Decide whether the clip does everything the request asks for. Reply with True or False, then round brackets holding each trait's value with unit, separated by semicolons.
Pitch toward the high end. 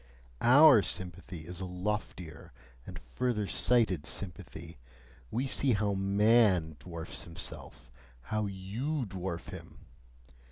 False (95 Hz)